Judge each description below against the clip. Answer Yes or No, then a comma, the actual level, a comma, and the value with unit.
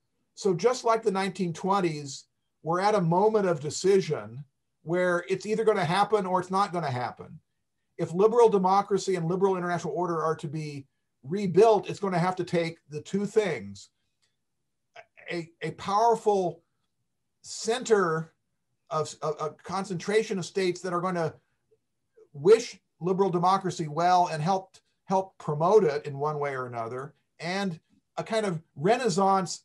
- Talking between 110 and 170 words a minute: Yes, average, 155 wpm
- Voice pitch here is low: No, medium, 180 Hz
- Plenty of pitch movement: No, average, 3.9 semitones